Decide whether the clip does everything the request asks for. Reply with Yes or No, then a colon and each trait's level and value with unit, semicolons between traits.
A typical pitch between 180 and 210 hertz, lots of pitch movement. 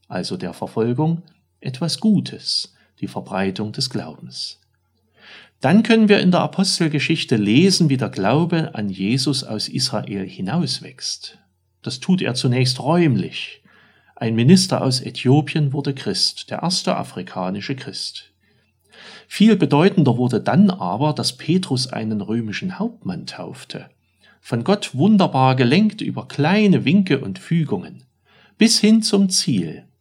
No: medium, 150 Hz; wide, 6.9 semitones